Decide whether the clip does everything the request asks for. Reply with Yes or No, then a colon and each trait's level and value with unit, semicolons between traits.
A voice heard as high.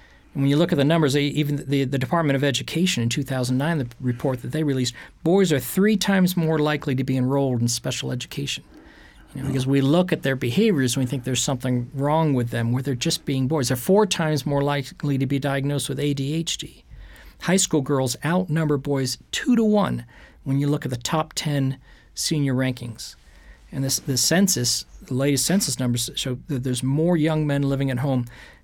No: medium, 140 Hz